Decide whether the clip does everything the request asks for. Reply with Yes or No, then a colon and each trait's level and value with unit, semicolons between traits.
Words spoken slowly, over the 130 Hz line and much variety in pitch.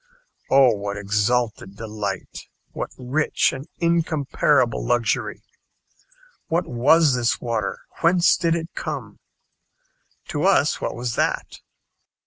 No: slow, 110 wpm; low, 125 Hz; wide, 6.2 semitones